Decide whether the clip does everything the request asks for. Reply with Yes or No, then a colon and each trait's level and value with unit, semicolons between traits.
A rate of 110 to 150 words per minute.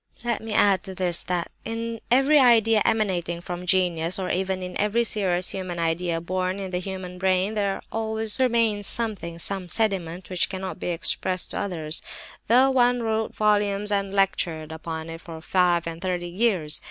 No: average, 160 wpm